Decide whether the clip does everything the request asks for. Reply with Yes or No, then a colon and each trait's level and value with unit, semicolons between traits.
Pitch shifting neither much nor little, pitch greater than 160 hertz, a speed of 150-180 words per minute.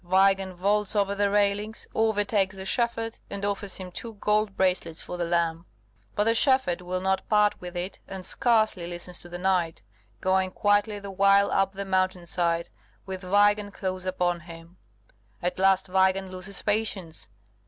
No: narrow, 2.3 semitones; high, 190 Hz; average, 165 wpm